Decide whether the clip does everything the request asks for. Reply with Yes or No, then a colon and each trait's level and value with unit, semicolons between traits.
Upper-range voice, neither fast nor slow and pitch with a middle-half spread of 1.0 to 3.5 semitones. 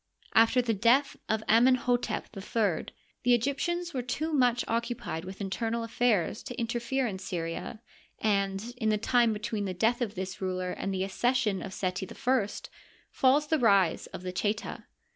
No: high, 225 Hz; average, 170 wpm; average, 4.1 semitones